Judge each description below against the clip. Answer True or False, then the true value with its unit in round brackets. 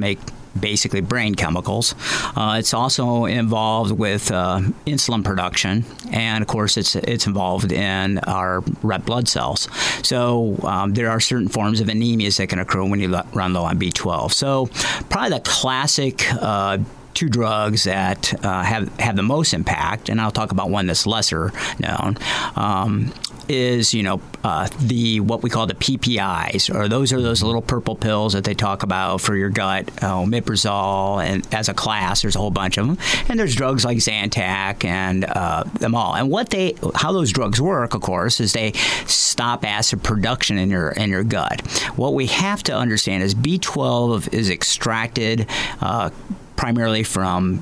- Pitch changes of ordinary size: True (3.5 semitones)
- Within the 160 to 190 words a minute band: True (175 wpm)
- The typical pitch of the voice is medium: False (110 Hz)